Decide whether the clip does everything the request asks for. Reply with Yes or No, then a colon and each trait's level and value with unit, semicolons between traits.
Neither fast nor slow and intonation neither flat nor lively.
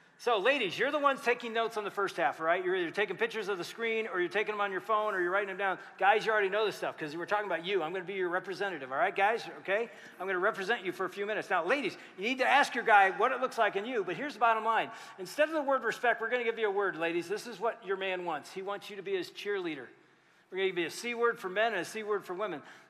No: fast, 320 wpm; average, 3.4 semitones